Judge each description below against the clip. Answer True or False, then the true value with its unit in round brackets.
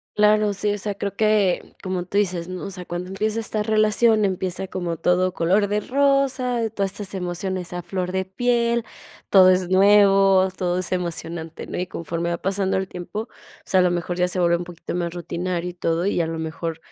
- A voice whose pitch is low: False (185 Hz)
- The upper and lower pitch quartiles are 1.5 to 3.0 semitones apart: True (2.7 semitones)